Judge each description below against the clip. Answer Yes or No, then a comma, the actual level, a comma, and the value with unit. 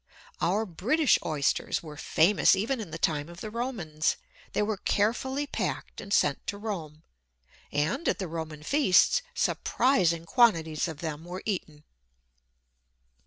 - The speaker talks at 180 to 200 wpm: No, average, 140 wpm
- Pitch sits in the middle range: Yes, medium, 180 Hz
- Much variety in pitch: Yes, wide, 5.8 semitones